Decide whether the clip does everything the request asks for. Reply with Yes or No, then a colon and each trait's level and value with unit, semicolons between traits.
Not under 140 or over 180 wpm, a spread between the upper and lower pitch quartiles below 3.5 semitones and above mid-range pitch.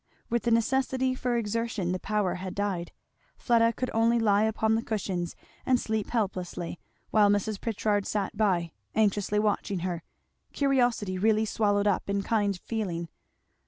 Yes: average, 150 wpm; average, 2.7 semitones; high, 210 Hz